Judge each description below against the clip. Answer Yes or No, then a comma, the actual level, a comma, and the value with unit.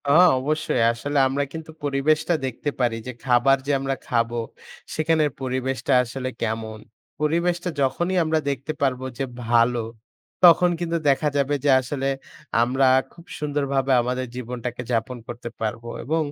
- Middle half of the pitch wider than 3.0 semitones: Yes, average, 3.7 semitones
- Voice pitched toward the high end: No, low, 135 Hz